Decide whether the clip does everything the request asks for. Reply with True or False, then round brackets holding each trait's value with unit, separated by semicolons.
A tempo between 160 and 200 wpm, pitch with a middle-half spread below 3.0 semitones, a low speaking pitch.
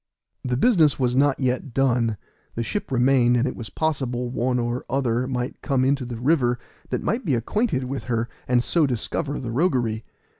True (185 wpm; 2.4 semitones; 125 Hz)